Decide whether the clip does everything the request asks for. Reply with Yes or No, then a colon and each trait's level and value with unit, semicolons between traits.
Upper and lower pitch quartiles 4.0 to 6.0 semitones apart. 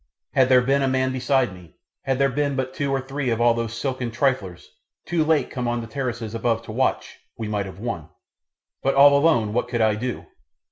No: average, 2.9 semitones